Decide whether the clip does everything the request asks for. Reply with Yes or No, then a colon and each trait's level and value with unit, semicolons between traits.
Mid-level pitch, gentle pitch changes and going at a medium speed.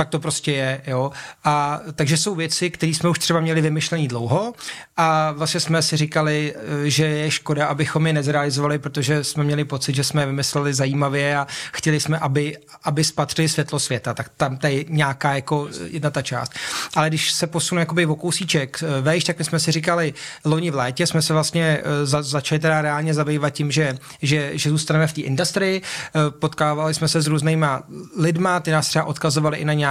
No: medium, 155 Hz; narrow, 1.6 semitones; fast, 195 wpm